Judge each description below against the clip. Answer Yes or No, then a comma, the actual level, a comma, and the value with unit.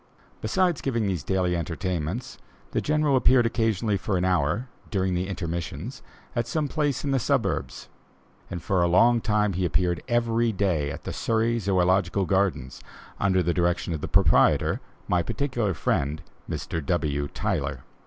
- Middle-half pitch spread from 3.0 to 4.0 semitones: No, average, 5.1 semitones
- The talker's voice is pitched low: Yes, very low, 95 Hz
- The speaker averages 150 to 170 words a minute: Yes, average, 155 wpm